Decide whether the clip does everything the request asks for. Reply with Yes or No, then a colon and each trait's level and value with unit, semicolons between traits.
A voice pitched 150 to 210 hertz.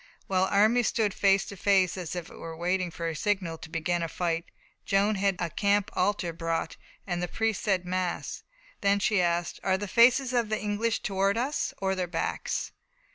Yes: high, 190 Hz